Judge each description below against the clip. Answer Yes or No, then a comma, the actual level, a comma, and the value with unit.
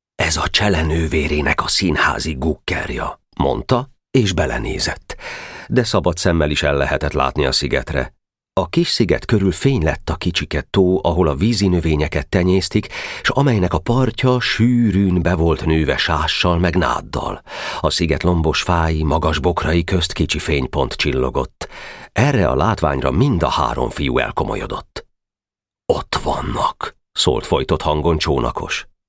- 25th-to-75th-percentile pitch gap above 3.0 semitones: Yes, average, 4.0 semitones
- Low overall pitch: Yes, very low, 85 Hz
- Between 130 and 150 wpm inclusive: Yes, average, 140 wpm